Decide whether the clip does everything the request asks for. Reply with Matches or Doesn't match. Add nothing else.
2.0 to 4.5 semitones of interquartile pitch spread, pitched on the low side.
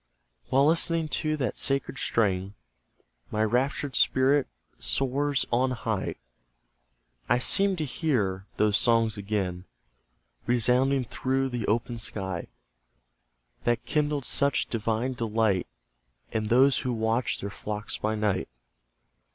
Matches